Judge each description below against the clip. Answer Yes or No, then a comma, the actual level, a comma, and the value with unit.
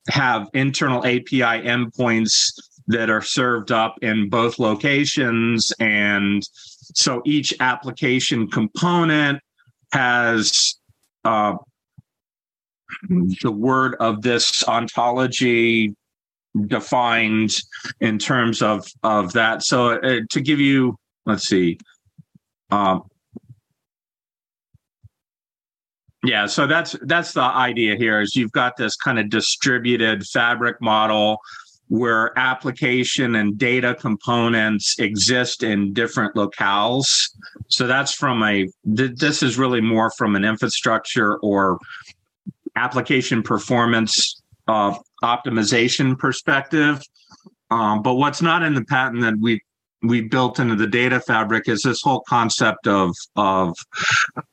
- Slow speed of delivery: Yes, slow, 110 wpm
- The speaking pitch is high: No, low, 120 Hz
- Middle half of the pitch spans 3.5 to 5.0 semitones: No, average, 3.0 semitones